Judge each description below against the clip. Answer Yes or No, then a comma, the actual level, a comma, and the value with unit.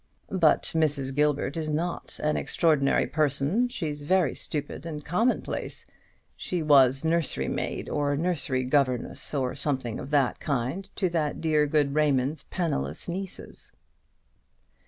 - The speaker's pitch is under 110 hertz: No, medium, 150 Hz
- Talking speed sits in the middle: No, slow, 130 wpm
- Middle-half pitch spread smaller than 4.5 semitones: Yes, average, 3.1 semitones